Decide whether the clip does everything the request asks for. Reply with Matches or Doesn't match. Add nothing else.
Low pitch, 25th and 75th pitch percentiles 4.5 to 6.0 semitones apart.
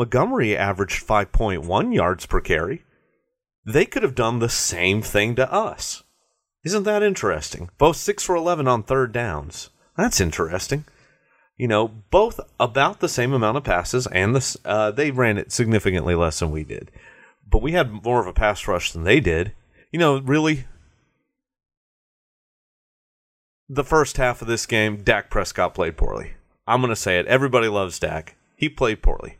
Matches